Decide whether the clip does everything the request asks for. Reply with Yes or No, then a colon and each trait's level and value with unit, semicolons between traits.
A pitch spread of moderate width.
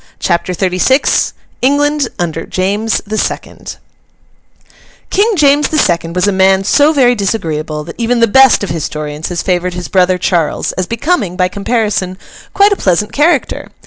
No: wide, 6.7 semitones